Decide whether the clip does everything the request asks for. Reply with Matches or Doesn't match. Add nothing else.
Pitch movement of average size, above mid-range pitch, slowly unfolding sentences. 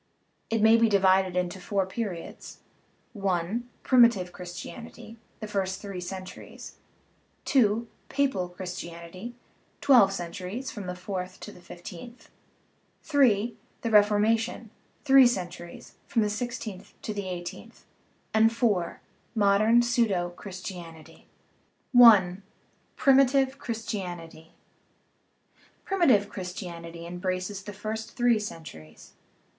Matches